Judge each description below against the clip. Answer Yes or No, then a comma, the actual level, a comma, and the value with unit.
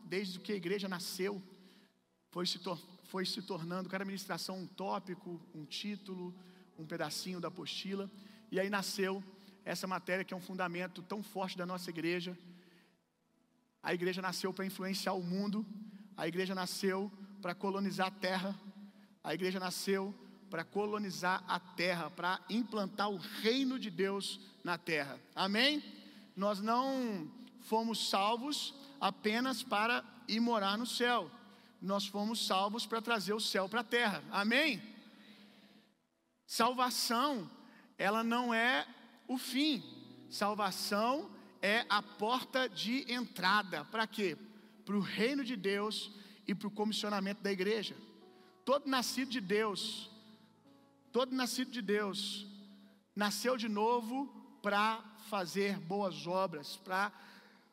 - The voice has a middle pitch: No, high, 205 Hz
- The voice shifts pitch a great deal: No, average, 3.2 semitones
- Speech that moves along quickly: No, average, 130 wpm